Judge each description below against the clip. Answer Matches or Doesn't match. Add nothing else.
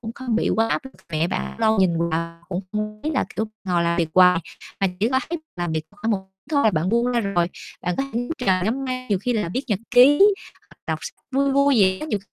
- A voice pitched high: Matches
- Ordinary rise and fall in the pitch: Doesn't match